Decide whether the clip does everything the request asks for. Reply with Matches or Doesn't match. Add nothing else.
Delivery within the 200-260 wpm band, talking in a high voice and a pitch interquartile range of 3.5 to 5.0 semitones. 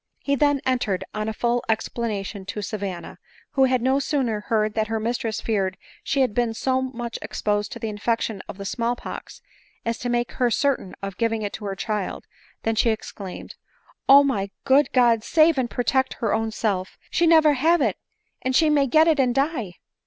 Matches